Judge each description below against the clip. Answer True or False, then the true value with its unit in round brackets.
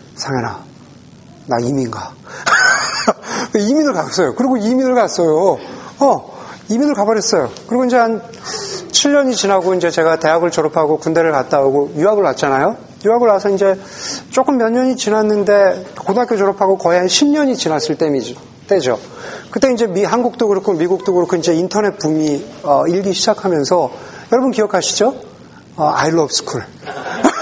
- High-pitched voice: True (195 Hz)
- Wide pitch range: True (6.1 semitones)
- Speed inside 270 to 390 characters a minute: True (340 characters per minute)